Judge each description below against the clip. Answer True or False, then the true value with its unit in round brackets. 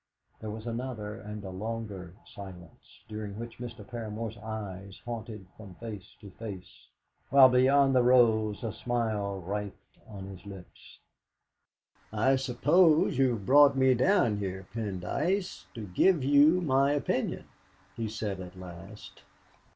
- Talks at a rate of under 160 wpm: True (135 wpm)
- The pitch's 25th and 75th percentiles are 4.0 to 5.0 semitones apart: True (4.3 semitones)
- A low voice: True (110 Hz)